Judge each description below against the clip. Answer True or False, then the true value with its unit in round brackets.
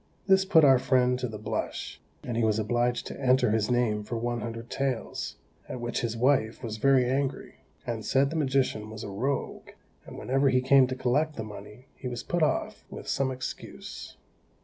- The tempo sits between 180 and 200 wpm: True (195 wpm)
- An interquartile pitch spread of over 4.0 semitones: False (2.9 semitones)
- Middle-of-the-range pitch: False (125 Hz)